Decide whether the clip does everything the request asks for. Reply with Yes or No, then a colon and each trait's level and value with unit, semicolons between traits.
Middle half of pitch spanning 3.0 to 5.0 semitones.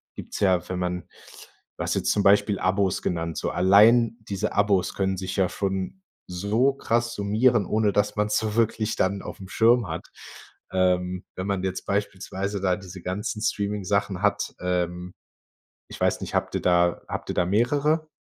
No: narrow, 2.5 semitones